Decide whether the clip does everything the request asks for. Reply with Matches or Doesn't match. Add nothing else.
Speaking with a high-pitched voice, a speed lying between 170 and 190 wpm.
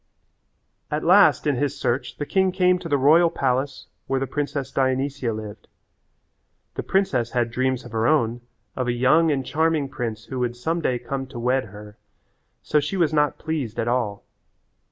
Doesn't match